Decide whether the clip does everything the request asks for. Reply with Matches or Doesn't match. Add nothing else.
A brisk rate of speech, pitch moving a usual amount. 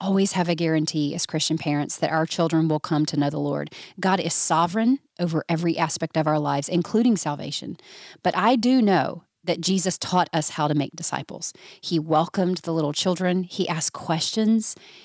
Doesn't match